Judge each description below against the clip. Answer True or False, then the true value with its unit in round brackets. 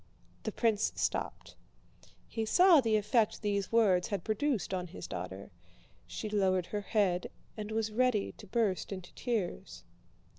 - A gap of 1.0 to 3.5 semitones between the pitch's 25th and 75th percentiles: True (2.8 semitones)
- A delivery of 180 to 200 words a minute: False (145 wpm)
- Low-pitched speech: False (210 Hz)